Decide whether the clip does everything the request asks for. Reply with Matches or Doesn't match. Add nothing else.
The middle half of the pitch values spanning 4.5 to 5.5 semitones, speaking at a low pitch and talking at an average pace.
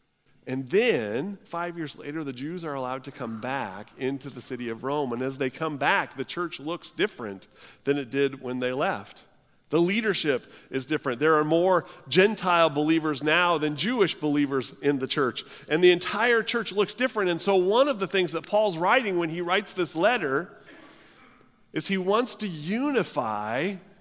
Doesn't match